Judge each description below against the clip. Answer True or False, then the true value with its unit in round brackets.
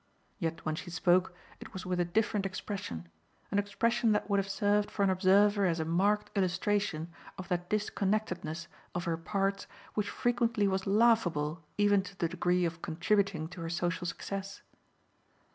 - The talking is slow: False (165 wpm)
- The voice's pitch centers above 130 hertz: True (190 Hz)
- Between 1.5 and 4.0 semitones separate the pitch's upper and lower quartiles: True (2.9 semitones)